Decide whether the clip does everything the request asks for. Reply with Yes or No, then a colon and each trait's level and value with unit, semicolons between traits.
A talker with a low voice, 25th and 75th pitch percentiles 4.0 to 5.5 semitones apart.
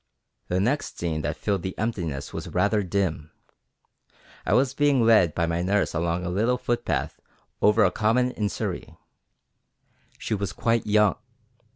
Yes: low, 100 Hz; average, 4.7 semitones